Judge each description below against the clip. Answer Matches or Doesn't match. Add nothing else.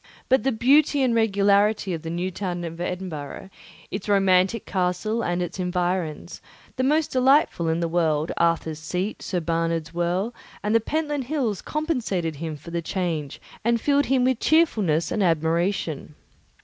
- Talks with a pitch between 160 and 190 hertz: Matches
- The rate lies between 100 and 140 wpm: Doesn't match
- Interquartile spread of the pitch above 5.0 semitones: Matches